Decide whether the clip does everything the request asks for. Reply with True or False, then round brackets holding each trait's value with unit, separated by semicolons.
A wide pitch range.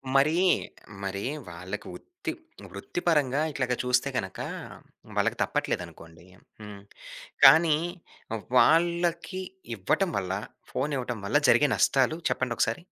True (7.8 semitones)